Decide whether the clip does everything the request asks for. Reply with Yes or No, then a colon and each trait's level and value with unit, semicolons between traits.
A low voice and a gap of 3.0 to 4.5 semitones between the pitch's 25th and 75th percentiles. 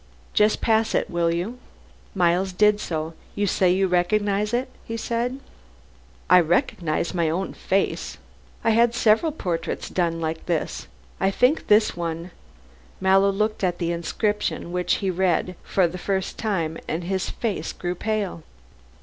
No: high, 190 Hz; average, 3.7 semitones